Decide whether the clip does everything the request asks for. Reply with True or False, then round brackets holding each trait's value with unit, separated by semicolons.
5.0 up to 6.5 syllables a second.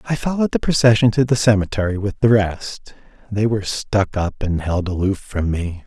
True (5.3 syllables/s)